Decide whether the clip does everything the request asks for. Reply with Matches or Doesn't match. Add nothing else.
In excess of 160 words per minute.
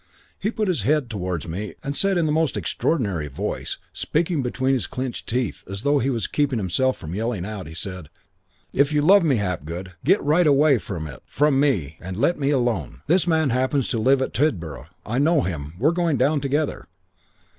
Matches